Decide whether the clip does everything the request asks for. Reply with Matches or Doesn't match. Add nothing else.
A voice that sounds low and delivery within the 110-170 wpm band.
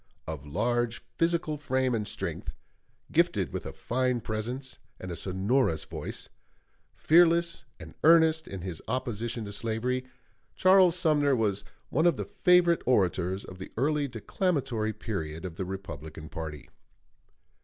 Matches